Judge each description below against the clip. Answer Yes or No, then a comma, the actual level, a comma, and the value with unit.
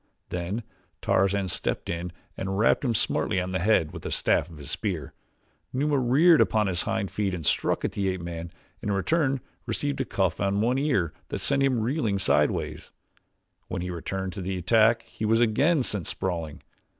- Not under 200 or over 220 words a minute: No, average, 190 wpm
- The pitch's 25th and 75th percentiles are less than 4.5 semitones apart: No, average, 5.0 semitones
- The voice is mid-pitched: No, low, 100 Hz